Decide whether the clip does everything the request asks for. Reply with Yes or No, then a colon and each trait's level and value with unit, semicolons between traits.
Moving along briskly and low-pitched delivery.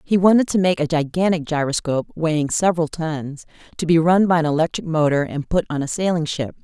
No: fast, 210 wpm; medium, 160 Hz